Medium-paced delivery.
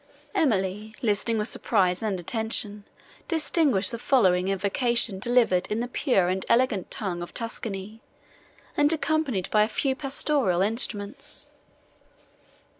No: slow, 120 wpm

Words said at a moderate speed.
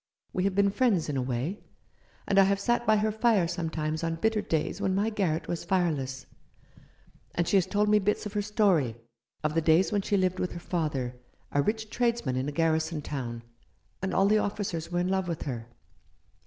No: fast, 210 wpm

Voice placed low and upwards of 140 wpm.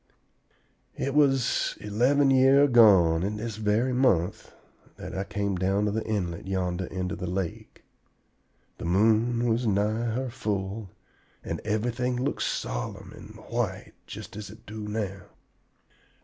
No: low, 105 Hz; slow, 135 wpm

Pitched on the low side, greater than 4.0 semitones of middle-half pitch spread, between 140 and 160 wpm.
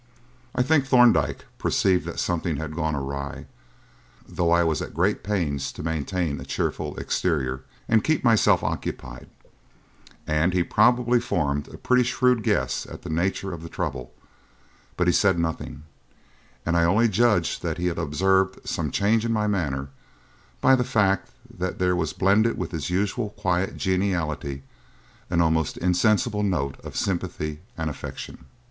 Yes: very low, 90 Hz; average, 4.9 semitones; average, 155 wpm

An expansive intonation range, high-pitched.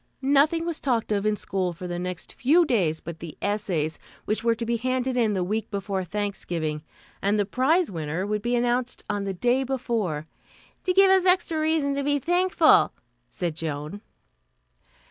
Yes: wide, 7.1 semitones; high, 215 Hz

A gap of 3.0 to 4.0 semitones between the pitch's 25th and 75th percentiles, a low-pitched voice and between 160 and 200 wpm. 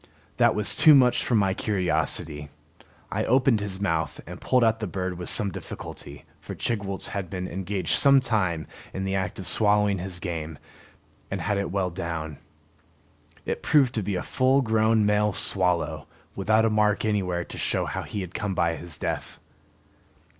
Yes: average, 3.5 semitones; low, 100 Hz; average, 175 wpm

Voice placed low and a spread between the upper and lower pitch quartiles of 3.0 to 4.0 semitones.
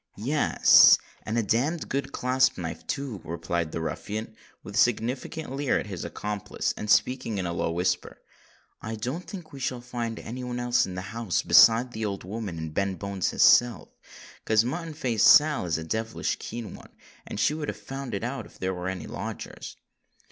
No: low, 115 Hz; average, 4.9 semitones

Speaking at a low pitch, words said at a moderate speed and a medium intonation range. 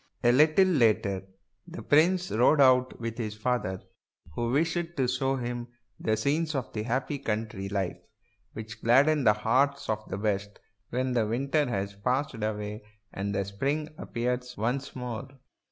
Yes: low, 120 Hz; average, 150 wpm; average, 4.4 semitones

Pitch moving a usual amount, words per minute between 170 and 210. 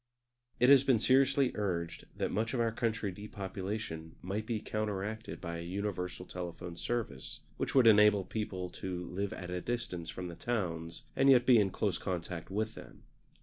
Yes: average, 4.2 semitones; average, 175 wpm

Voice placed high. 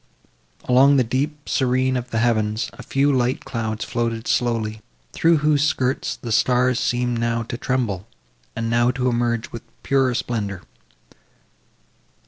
No: low, 120 Hz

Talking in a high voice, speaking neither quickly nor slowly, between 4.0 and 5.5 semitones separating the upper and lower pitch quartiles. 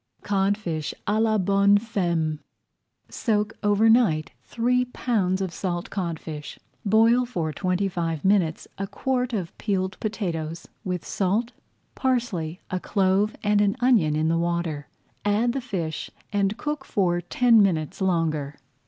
Yes: high, 195 Hz; average, 145 wpm; average, 4.4 semitones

